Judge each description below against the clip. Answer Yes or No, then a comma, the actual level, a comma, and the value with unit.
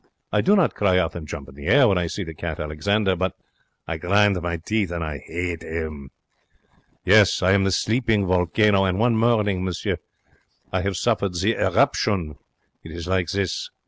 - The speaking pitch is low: Yes, very low, 95 Hz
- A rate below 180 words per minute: No, average, 190 wpm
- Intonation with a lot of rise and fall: No, average, 3.6 semitones